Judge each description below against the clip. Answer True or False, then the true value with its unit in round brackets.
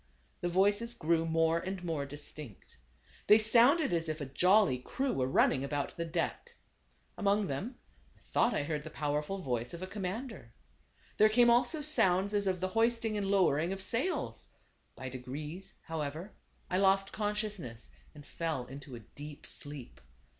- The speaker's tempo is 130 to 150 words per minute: False (165 wpm)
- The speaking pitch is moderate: True (175 Hz)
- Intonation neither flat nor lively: False (6.1 semitones)